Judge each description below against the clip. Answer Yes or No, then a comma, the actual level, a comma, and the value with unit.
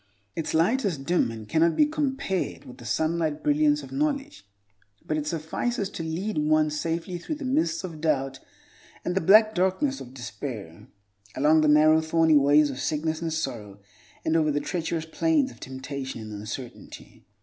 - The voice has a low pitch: No, medium, 160 Hz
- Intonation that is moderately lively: Yes, average, 4.9 semitones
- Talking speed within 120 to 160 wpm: No, average, 170 wpm